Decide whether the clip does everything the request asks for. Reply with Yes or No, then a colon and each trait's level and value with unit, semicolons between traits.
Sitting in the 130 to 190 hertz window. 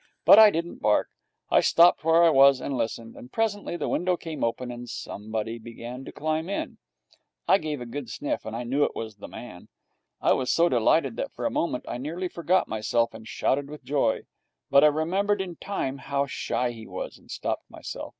Yes: medium, 140 Hz